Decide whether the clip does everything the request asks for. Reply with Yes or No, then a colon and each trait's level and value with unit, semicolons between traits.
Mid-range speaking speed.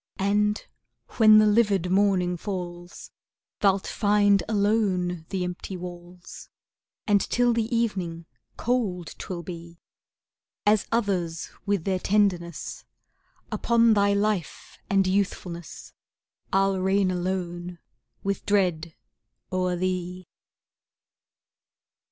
No: slow, 100 wpm